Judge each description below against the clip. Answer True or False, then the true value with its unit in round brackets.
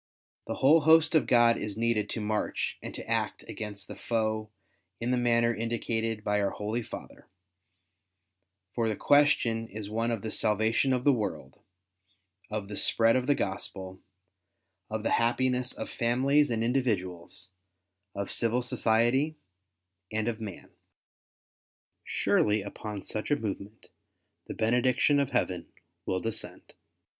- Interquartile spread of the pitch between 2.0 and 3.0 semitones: True (2.7 semitones)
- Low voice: True (115 Hz)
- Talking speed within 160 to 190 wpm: False (145 wpm)